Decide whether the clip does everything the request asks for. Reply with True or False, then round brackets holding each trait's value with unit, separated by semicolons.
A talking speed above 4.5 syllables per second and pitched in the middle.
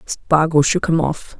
False (3.9 syllables/s; 155 Hz)